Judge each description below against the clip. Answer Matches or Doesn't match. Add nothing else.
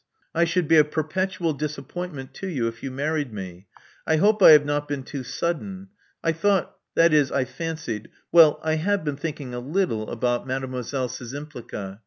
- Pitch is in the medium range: Matches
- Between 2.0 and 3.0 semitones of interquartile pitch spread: Doesn't match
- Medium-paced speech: Matches